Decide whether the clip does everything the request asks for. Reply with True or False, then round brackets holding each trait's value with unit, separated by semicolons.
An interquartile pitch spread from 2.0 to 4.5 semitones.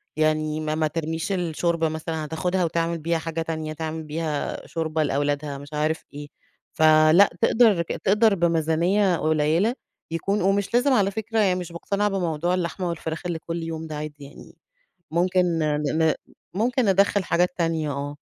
True (2.8 semitones)